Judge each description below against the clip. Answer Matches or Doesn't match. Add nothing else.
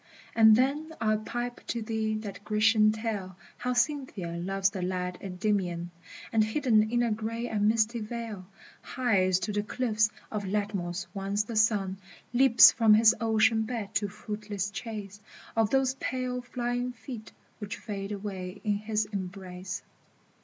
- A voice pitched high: Matches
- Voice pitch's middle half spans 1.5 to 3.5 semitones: Matches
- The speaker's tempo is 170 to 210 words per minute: Doesn't match